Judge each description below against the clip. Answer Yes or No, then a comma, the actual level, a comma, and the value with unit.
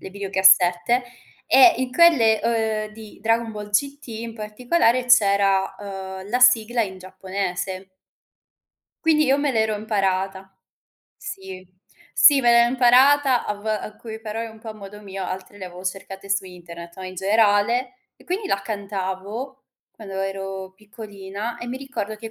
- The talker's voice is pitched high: Yes, high, 210 Hz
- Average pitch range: Yes, average, 3.6 semitones